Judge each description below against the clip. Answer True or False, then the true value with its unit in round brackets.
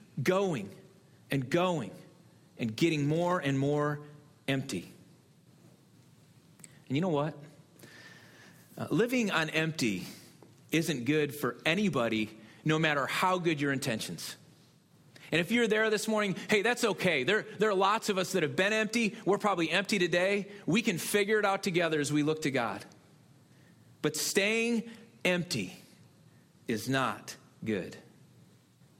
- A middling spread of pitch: False (5.7 semitones)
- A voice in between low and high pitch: True (165 Hz)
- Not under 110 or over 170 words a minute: True (140 wpm)